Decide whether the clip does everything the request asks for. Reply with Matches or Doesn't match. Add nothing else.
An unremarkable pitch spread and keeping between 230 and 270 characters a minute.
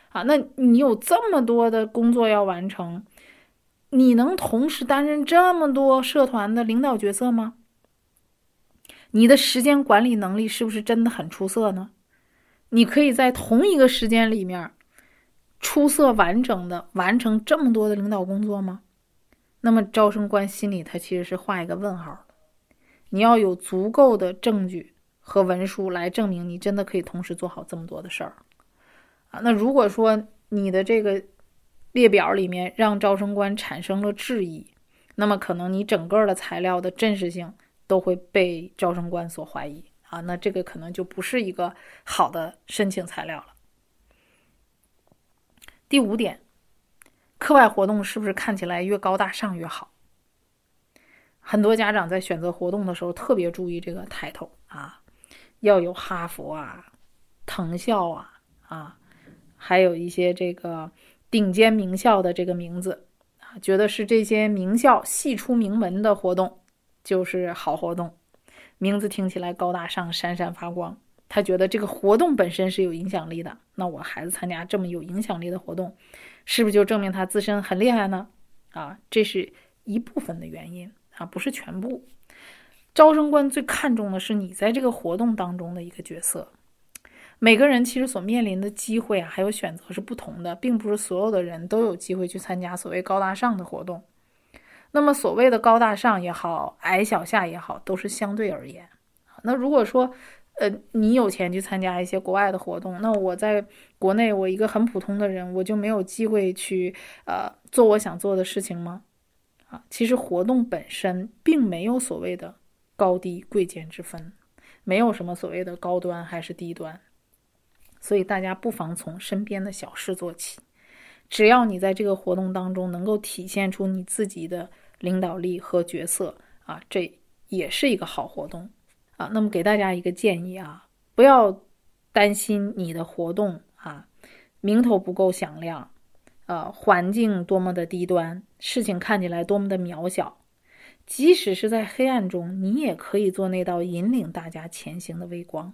Matches